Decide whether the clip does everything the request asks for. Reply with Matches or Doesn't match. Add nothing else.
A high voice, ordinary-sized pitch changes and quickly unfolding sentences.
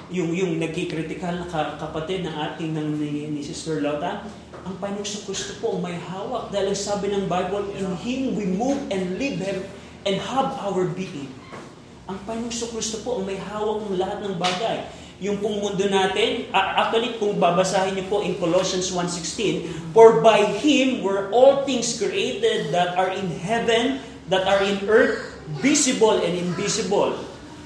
Matches